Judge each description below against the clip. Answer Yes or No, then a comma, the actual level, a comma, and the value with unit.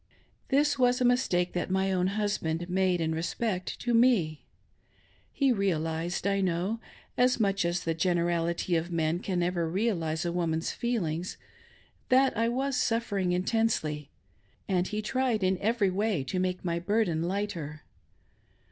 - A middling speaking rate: Yes, average, 155 wpm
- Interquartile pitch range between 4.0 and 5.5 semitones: Yes, average, 4.7 semitones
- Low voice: No, medium, 185 Hz